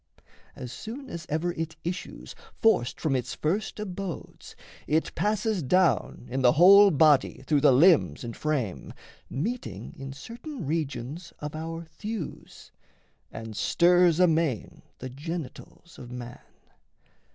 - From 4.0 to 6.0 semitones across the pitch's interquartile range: Yes, wide, 5.5 semitones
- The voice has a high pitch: No, medium, 160 Hz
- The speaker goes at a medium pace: No, slow, 130 wpm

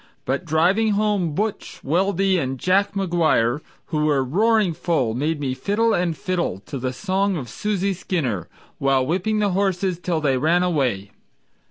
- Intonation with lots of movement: Yes, wide, 6.2 semitones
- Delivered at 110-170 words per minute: Yes, average, 160 wpm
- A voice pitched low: No, medium, 175 Hz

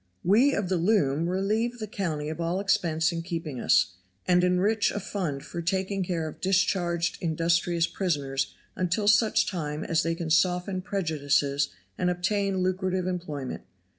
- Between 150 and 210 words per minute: Yes, average, 155 wpm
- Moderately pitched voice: Yes, medium, 180 Hz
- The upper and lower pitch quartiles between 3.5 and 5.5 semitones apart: No, average, 3.0 semitones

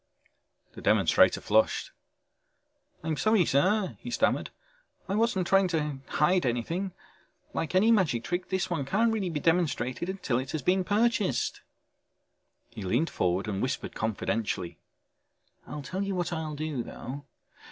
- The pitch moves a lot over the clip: Yes, wide, 6.3 semitones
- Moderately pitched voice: Yes, medium, 165 Hz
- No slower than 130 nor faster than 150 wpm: Yes, average, 140 wpm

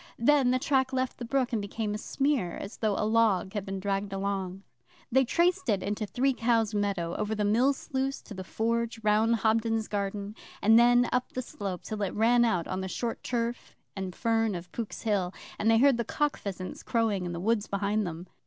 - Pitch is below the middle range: No, high, 220 Hz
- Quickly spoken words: Yes, fast, 210 wpm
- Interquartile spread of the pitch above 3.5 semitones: No, average, 3.2 semitones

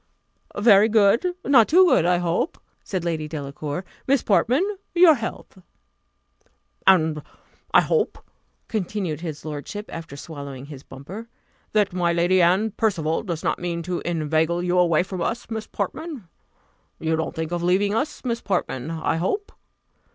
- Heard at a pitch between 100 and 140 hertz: No, medium, 180 Hz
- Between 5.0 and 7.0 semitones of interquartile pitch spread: Yes, average, 5.3 semitones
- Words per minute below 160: Yes, average, 150 wpm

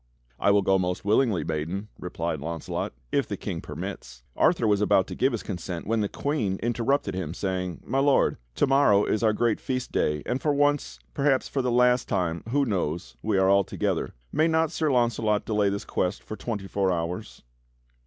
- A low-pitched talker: Yes, low, 105 Hz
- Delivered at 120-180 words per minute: No, average, 200 wpm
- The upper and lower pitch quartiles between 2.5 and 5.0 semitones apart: No, wide, 5.4 semitones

